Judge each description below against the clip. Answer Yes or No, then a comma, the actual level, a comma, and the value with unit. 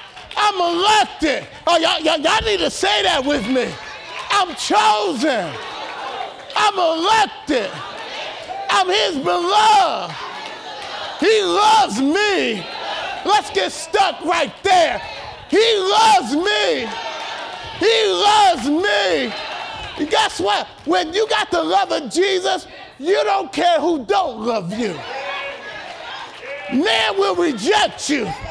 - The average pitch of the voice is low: No, very high, 370 Hz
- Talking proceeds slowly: Yes, slow, 115 wpm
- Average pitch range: Yes, average, 4.6 semitones